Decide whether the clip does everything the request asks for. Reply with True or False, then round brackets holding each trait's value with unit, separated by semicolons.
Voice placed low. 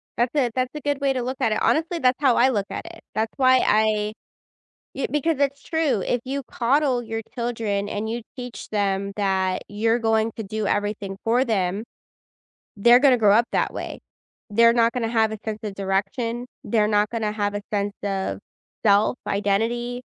False (225 Hz)